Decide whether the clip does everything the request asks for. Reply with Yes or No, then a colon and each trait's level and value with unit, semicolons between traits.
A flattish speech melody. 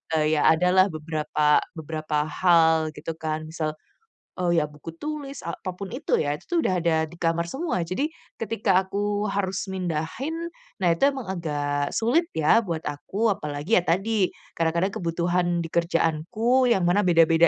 No: average, 3.1 semitones